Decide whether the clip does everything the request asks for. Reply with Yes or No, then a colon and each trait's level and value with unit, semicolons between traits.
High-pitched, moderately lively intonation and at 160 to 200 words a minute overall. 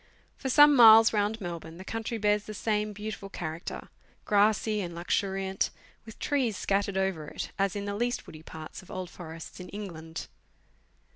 Yes: high, 200 Hz; average, 3.6 semitones; average, 165 wpm